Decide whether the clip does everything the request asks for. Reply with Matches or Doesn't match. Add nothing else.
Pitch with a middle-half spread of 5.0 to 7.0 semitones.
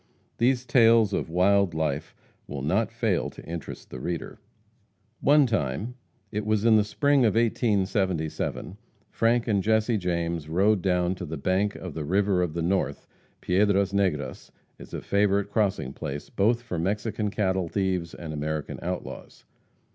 Doesn't match